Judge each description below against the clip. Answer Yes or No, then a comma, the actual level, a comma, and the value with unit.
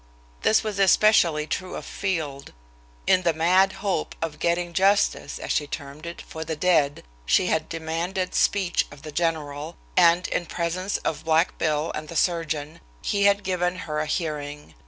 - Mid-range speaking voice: Yes, medium, 165 Hz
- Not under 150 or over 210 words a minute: Yes, average, 170 wpm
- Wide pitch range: No, average, 3.1 semitones